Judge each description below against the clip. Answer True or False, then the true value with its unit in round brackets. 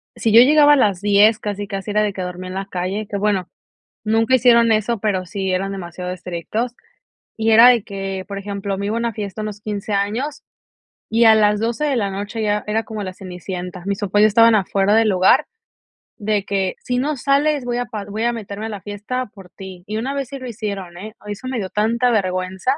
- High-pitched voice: True (210 Hz)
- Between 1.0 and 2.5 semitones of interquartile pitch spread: False (2.9 semitones)